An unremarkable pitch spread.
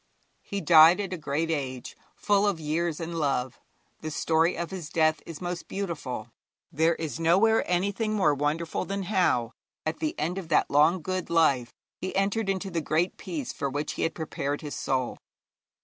Yes: average, 3.8 semitones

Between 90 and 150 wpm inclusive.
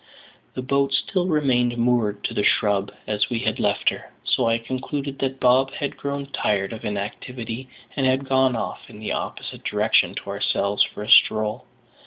No: average, 180 wpm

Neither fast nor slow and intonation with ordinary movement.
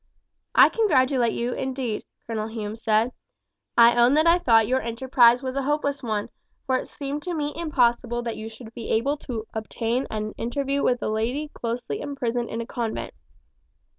Yes: average, 175 wpm; average, 3.3 semitones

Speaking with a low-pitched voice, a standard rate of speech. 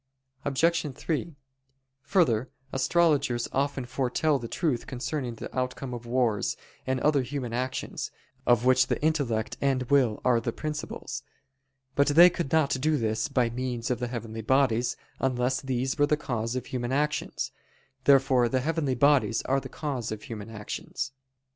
Yes: low, 130 Hz; average, 155 wpm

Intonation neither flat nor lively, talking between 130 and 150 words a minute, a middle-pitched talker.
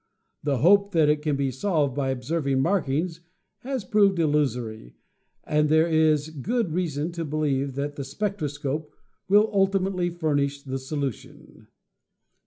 Yes: average, 4.1 semitones; average, 145 wpm; medium, 150 Hz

